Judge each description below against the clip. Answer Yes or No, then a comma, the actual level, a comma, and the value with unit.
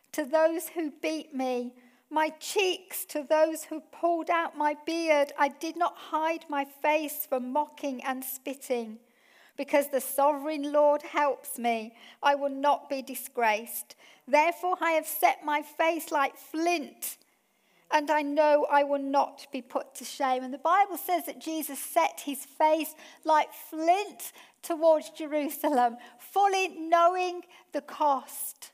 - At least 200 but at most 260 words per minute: No, average, 145 wpm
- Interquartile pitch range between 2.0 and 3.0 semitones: Yes, narrow, 2.6 semitones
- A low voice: No, very high, 300 Hz